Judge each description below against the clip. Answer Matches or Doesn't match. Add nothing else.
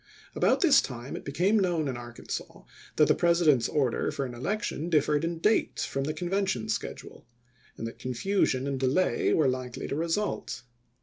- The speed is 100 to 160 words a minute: Doesn't match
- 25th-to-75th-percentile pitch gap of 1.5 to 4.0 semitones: Doesn't match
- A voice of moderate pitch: Matches